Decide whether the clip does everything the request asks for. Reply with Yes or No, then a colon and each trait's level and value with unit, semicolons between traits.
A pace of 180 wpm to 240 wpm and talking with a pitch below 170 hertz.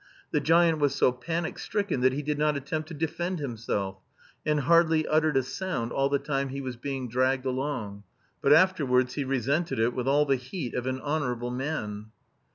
Yes: average, 190 wpm; medium, 140 Hz